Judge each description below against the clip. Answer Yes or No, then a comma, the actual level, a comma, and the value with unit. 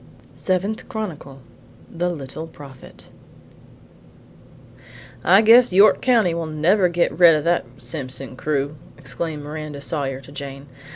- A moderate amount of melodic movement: Yes, average, 4.1 semitones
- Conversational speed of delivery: No, slow, 125 wpm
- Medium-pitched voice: Yes, medium, 155 Hz